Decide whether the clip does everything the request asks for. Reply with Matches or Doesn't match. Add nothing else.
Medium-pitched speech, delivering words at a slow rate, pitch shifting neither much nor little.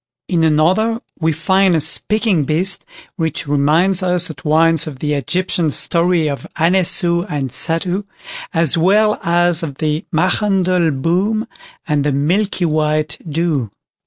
Matches